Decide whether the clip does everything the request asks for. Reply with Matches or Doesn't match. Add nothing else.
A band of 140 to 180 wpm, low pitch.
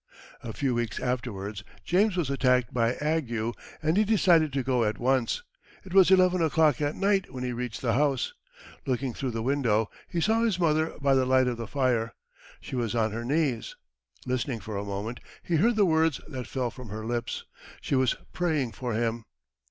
Doesn't match